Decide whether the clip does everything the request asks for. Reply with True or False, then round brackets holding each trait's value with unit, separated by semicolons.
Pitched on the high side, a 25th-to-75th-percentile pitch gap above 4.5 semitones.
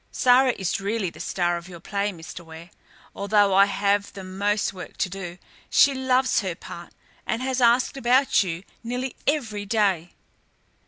True (200 Hz; 5.0 semitones)